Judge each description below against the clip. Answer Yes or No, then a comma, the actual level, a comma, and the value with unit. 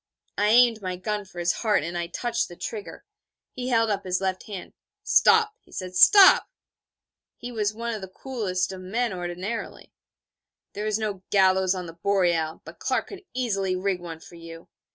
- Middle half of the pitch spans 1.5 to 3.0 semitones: No, average, 3.8 semitones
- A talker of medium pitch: No, high, 195 Hz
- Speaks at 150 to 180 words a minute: No, average, 190 wpm